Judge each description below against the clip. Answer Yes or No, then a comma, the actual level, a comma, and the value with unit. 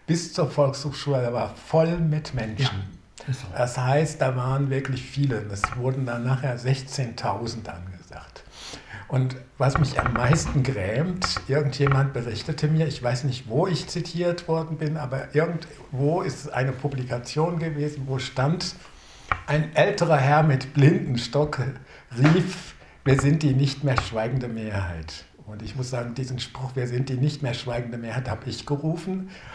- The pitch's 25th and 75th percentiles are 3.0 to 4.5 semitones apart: Yes, average, 3.6 semitones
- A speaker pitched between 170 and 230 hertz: No, low, 135 Hz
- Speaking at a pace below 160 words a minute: Yes, average, 150 wpm